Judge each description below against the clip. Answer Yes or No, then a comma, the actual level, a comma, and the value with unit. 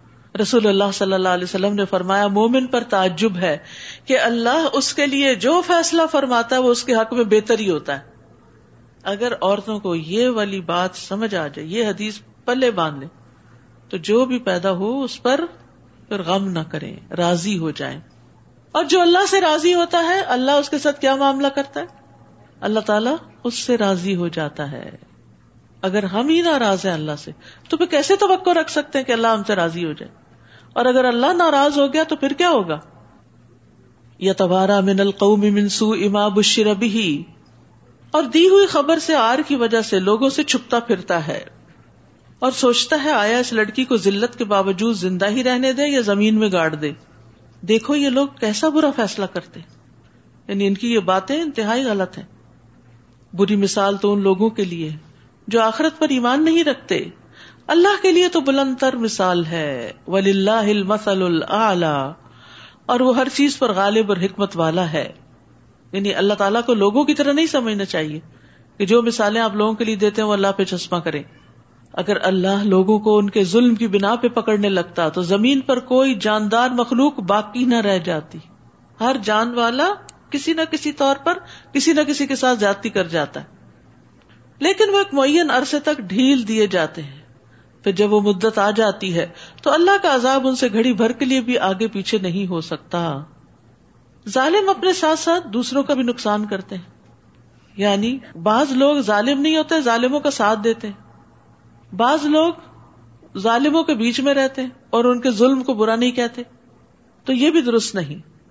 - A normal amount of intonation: No, wide, 6.0 semitones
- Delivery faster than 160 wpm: Yes, average, 185 wpm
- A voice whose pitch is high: Yes, high, 220 Hz